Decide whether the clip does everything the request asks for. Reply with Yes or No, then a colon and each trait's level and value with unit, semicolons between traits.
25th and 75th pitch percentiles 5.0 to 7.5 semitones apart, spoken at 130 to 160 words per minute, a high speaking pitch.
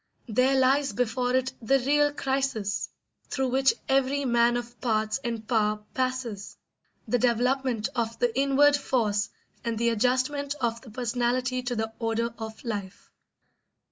No: average, 2.7 semitones; average, 140 wpm; high, 245 Hz